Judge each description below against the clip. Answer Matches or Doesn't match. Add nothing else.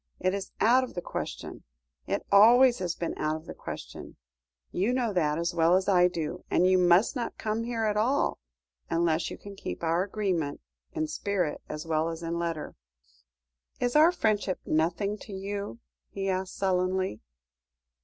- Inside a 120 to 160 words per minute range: Doesn't match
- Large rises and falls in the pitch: Doesn't match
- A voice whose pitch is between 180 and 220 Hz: Matches